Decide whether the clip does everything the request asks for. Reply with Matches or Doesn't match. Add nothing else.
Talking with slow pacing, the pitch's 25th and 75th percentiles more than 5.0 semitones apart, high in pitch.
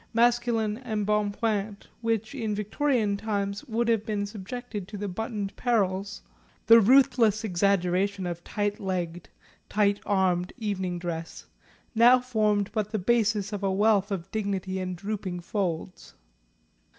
Doesn't match